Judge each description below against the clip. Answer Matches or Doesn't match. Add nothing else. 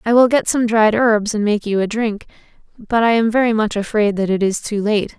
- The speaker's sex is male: Doesn't match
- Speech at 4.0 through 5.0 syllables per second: Doesn't match